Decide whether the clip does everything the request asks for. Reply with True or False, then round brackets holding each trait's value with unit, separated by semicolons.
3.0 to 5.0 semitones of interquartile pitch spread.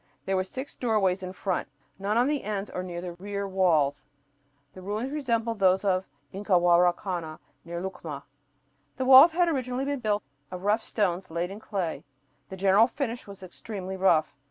True (3.8 semitones)